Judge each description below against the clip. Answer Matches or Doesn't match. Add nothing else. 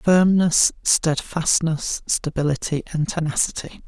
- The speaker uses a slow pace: Matches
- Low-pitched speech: Doesn't match